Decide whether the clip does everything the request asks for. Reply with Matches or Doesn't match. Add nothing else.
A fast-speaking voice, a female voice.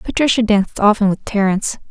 Doesn't match